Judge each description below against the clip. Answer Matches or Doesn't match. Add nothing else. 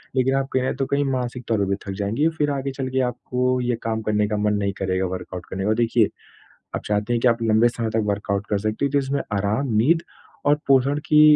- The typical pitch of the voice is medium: Doesn't match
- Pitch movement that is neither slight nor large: Matches